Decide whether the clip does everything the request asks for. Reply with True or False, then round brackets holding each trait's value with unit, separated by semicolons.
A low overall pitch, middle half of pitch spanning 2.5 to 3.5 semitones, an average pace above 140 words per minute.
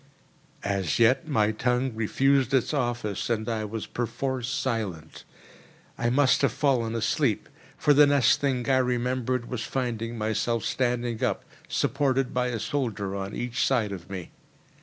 True (120 Hz; 3.1 semitones; 150 wpm)